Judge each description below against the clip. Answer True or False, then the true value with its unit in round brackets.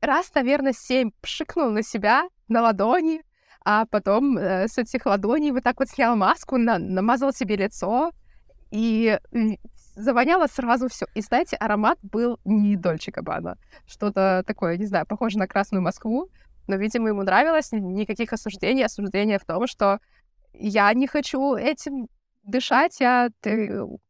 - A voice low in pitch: False (225 Hz)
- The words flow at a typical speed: True (150 wpm)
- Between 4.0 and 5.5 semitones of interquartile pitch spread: True (4.3 semitones)